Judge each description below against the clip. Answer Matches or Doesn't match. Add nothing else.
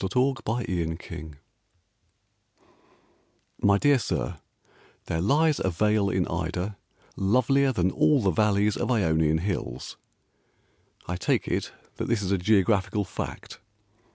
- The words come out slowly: Matches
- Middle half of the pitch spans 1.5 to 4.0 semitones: Doesn't match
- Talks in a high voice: Doesn't match